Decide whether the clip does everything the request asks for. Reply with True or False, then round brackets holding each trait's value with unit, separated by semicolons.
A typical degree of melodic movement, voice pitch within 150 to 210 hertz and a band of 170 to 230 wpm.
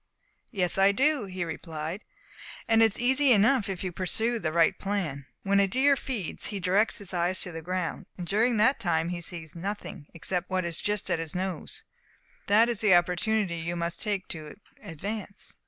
True (3.8 semitones; 190 Hz; 195 wpm)